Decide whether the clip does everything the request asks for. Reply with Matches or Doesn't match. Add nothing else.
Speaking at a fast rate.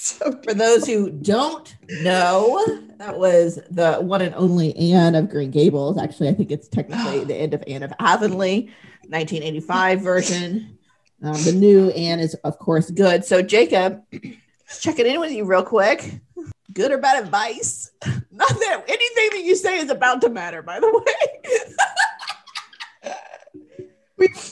Doesn't match